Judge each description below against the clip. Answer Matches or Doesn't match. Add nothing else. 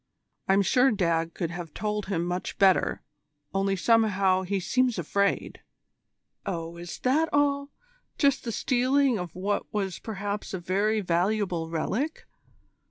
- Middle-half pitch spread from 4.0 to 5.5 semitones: Matches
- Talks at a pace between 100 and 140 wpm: Matches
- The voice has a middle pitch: Doesn't match